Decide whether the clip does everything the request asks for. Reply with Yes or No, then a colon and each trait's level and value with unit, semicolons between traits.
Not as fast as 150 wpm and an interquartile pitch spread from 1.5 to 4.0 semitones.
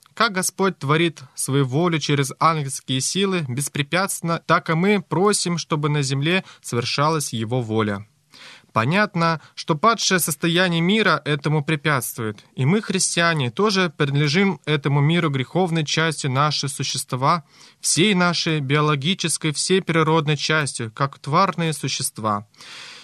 Yes: average, 120 wpm; average, 3.7 semitones